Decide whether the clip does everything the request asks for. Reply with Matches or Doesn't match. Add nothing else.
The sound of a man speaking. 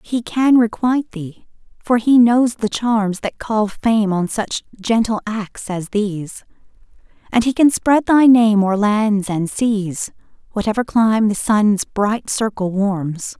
Doesn't match